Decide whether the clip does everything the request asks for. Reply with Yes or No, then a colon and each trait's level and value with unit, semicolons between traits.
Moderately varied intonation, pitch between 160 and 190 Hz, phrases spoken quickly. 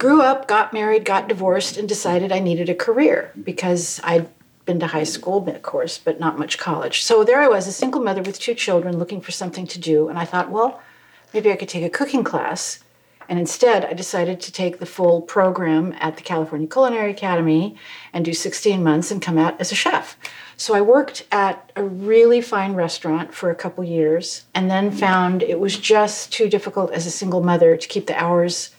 Yes: average, 3.8 semitones; medium, 185 Hz; fast, 215 wpm